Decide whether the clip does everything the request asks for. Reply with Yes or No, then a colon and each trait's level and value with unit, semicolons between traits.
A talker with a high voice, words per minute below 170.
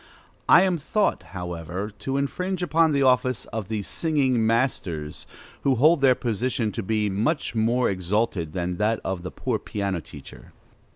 No: low, 115 Hz; average, 160 wpm